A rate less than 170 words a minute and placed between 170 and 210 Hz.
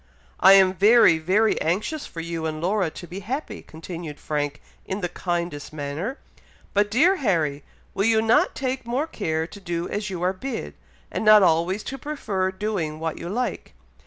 No: average, 180 wpm; high, 190 Hz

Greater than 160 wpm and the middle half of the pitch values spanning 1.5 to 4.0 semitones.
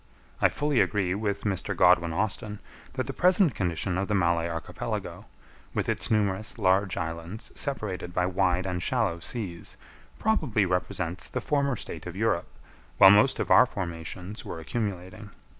No: average, 155 wpm; average, 3.5 semitones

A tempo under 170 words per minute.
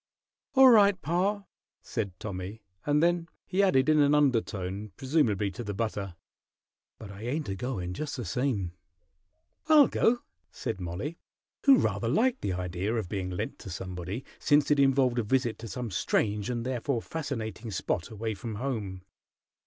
Yes: average, 160 wpm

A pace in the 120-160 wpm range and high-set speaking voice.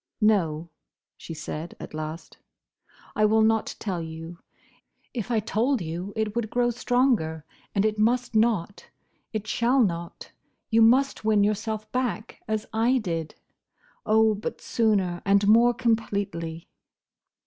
Yes: slow, 135 wpm; high, 215 Hz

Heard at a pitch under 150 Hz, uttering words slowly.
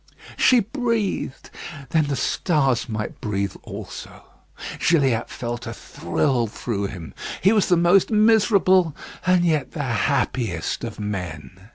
Yes: low, 135 Hz; slow, 130 wpm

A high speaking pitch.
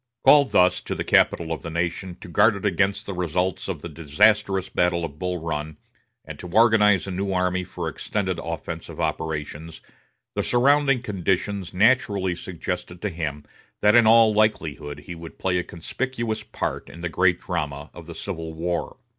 No: very low, 90 Hz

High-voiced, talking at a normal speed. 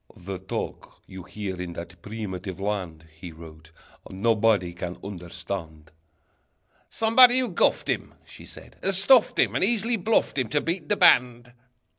No: low, 100 Hz; average, 150 wpm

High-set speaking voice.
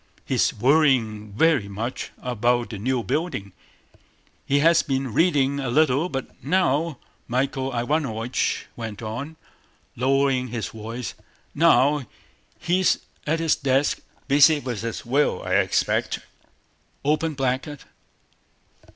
No: low, 135 Hz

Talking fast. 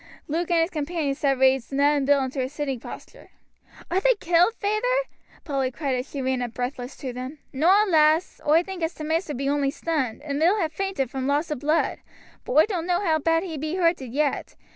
Yes: fast, 220 wpm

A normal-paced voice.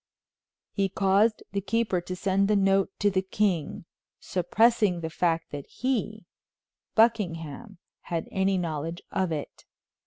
No: slow, 130 wpm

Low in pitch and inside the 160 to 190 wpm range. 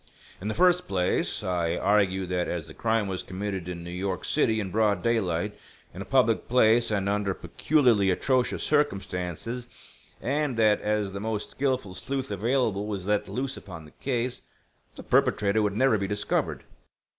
Yes: low, 105 Hz; average, 170 wpm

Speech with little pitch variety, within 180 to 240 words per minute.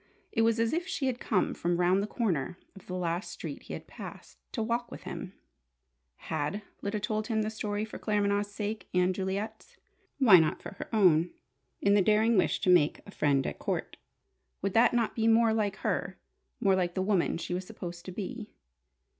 No: average, 3.5 semitones; average, 200 wpm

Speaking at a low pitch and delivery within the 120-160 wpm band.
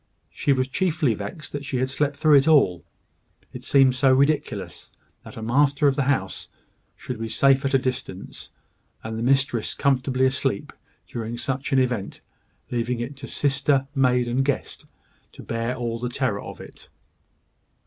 No: low, 130 Hz; average, 170 wpm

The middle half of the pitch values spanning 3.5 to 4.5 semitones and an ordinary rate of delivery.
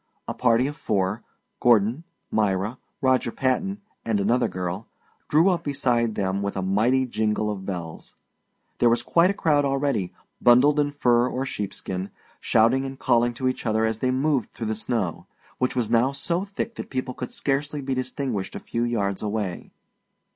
Yes: average, 4.1 semitones; average, 175 wpm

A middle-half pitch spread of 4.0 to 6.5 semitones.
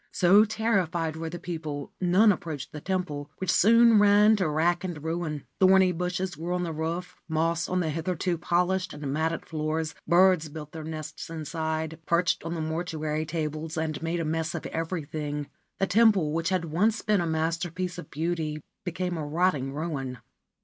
No: narrow, 2.5 semitones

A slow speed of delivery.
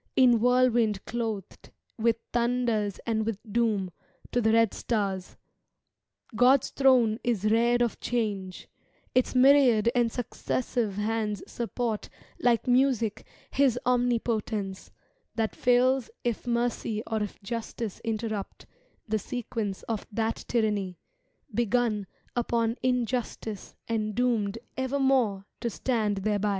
Yes: slow, 115 wpm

